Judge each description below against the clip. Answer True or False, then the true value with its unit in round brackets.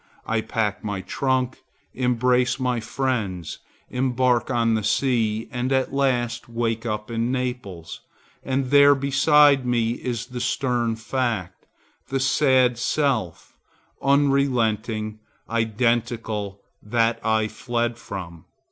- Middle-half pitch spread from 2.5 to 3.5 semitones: True (2.8 semitones)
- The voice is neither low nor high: False (120 Hz)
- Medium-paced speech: False (110 wpm)